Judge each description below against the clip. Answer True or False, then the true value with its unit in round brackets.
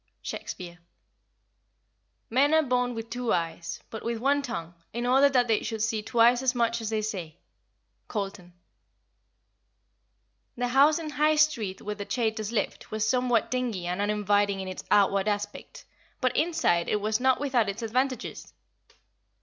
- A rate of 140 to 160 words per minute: True (155 wpm)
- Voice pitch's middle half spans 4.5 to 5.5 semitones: False (3.7 semitones)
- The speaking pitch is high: True (225 Hz)